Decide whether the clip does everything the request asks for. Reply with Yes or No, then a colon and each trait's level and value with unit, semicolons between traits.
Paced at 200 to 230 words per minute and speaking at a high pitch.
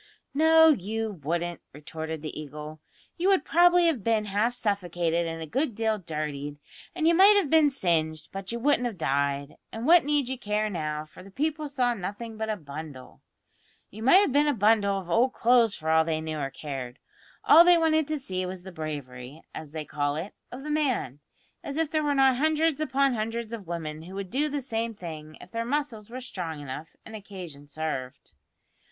Yes: fast, 205 wpm; high, 205 Hz